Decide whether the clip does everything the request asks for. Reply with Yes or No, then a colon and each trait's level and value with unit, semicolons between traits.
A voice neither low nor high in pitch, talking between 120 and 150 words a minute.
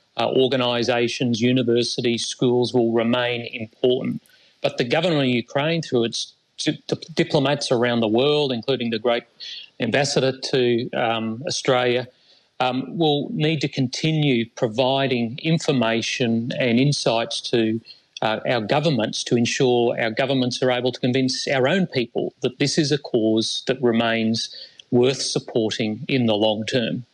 No: low, 125 Hz; average, 140 wpm